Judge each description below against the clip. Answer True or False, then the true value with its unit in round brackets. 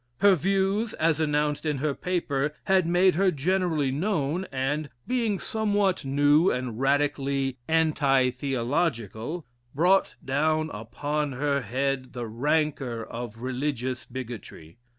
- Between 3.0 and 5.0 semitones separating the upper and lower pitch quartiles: True (4.5 semitones)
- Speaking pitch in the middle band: True (145 Hz)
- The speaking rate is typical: False (120 wpm)